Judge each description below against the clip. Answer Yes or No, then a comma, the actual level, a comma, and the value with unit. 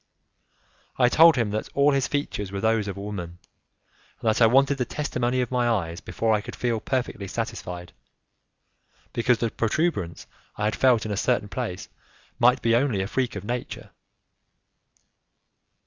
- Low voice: Yes, low, 115 Hz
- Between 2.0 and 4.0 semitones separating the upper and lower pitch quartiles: Yes, average, 3.6 semitones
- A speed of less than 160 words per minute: No, average, 165 wpm